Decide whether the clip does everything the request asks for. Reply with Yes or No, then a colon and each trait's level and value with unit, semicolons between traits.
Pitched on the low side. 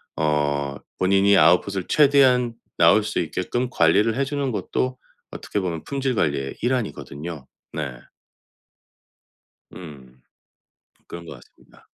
Yes: very low, 95 Hz